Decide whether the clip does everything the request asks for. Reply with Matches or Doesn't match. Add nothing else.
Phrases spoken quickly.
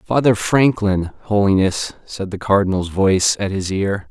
Doesn't match